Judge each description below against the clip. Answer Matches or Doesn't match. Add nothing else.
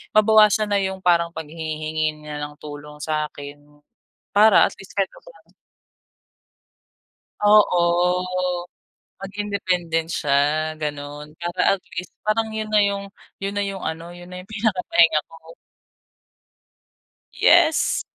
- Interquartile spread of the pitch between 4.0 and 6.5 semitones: Matches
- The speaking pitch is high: Doesn't match